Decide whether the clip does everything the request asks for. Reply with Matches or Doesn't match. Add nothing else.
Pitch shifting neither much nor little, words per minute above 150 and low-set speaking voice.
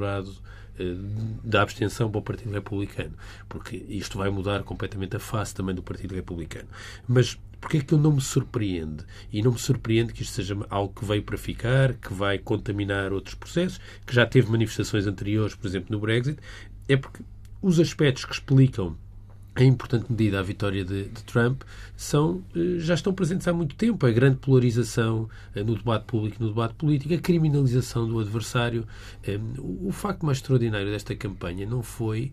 Matches